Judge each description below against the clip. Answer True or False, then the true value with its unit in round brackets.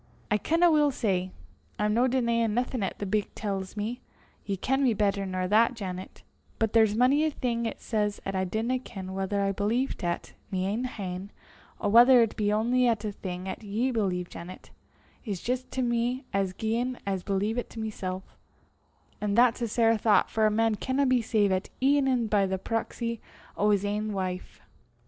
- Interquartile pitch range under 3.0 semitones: False (3.5 semitones)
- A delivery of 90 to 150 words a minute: False (190 wpm)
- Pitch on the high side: True (215 Hz)